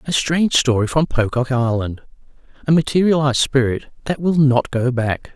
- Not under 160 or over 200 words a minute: No, average, 145 wpm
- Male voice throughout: Yes, male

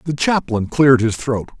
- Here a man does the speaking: Yes, male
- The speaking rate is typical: Yes, average, 190 wpm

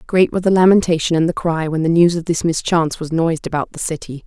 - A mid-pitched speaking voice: Yes, medium, 165 Hz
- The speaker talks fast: Yes, fast, 255 wpm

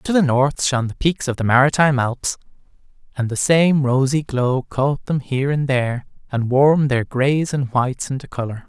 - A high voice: No, low, 135 Hz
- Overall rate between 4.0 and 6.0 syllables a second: Yes, 5.1 syllables/s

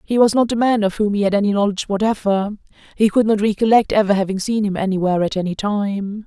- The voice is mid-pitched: No, high, 205 Hz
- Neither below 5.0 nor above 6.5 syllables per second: Yes, 6.4 syllables/s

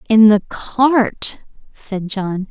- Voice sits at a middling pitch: No, high, 215 Hz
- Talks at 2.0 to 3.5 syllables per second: Yes, 2.6 syllables/s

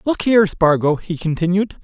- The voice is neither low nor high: Yes, medium, 180 Hz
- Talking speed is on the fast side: No, average, 165 wpm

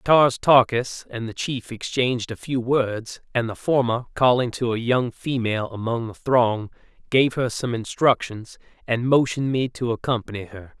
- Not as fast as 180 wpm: Yes, average, 165 wpm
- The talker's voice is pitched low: Yes, low, 120 Hz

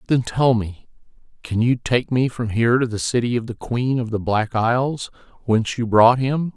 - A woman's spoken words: No, male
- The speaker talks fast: Yes, fast, 210 wpm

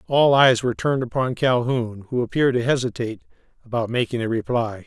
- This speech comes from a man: Yes, male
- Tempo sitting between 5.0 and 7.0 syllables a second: Yes, 6.1 syllables/s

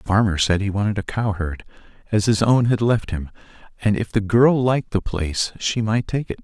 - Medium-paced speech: No, fast, 225 wpm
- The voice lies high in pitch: No, low, 105 Hz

